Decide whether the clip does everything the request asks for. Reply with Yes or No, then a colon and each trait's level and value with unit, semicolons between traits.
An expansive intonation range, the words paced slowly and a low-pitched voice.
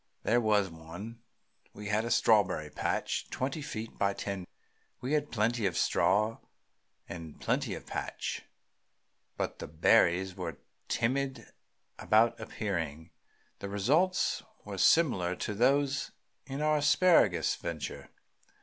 Yes: wide, 6.2 semitones; slow, 120 wpm; low, 110 Hz